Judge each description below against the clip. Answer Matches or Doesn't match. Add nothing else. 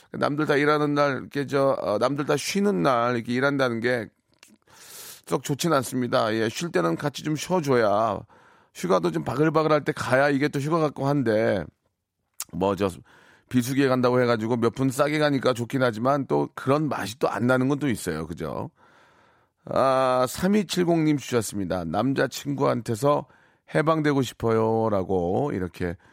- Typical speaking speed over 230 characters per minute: Matches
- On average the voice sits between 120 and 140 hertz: Matches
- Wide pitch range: Doesn't match